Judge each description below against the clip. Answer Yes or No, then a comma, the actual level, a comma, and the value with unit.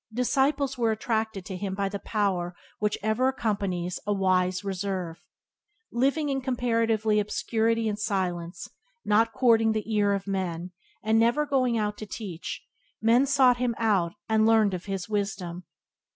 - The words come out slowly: No, average, 150 wpm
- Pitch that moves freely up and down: No, average, 3.1 semitones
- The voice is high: Yes, high, 215 Hz